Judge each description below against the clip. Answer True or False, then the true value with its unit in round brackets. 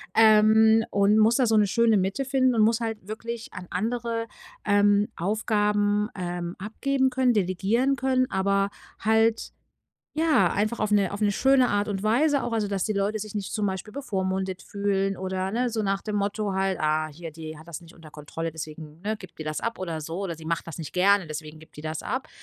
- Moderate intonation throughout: True (3.4 semitones)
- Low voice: False (205 Hz)